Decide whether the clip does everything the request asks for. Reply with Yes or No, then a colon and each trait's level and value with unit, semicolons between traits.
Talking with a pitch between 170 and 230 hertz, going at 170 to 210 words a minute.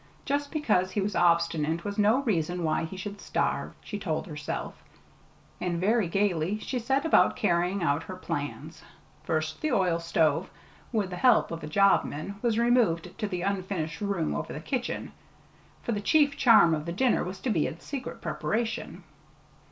Yes: high, 190 Hz; average, 175 wpm